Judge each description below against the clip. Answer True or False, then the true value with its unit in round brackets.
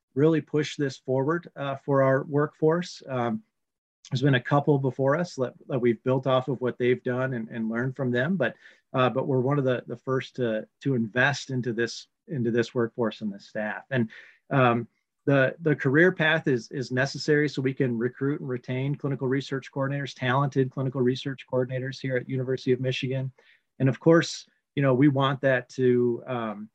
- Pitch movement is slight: True (2.1 semitones)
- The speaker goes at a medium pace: True (195 wpm)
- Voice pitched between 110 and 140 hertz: True (130 Hz)